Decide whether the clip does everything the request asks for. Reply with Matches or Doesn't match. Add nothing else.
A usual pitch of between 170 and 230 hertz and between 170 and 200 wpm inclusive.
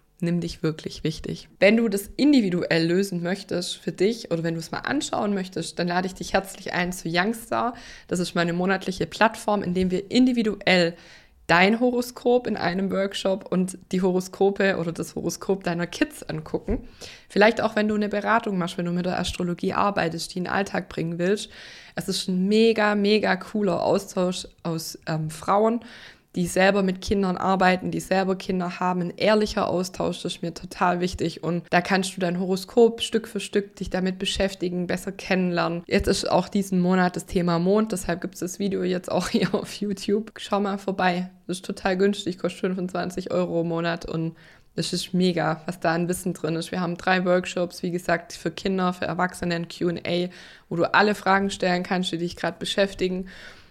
Matches